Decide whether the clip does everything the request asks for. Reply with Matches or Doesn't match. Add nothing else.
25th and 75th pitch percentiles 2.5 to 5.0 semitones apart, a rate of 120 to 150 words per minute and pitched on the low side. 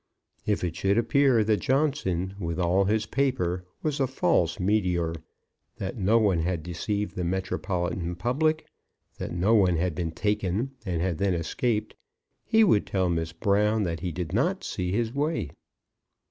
Doesn't match